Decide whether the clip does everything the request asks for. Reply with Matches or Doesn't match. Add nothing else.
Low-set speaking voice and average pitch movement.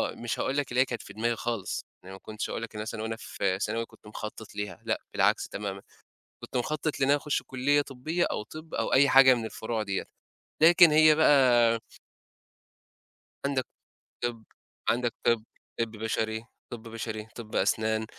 Matches